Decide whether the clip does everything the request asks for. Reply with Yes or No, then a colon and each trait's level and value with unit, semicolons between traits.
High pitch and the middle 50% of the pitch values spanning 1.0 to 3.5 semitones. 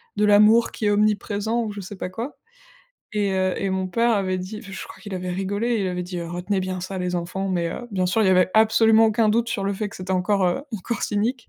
Yes: high, 200 Hz; average, 2.8 semitones